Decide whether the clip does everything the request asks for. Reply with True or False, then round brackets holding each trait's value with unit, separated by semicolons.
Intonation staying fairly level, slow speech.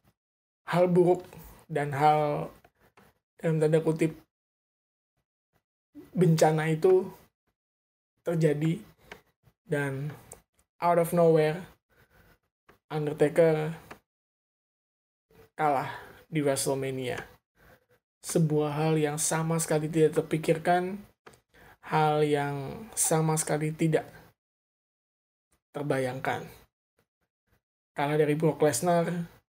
True (2.3 semitones; 70 wpm)